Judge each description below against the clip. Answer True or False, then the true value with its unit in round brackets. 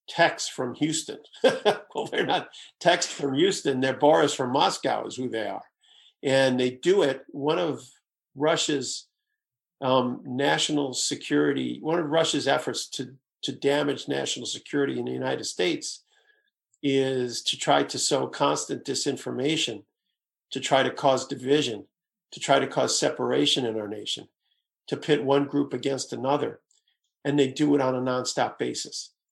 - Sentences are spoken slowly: False (150 wpm)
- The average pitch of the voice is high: False (140 Hz)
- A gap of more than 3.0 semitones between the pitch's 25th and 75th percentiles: False (2.5 semitones)